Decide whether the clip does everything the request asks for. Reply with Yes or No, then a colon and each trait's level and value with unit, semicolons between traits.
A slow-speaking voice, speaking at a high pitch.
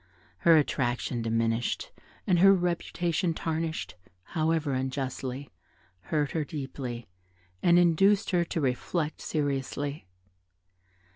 No: slow, 95 wpm; medium, 150 Hz